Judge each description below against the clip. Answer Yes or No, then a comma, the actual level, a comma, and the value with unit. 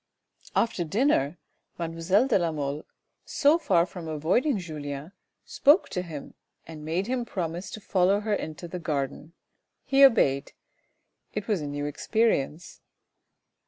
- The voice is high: No, medium, 175 Hz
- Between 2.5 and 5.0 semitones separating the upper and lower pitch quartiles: No, wide, 5.6 semitones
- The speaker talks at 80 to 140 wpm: Yes, slow, 135 wpm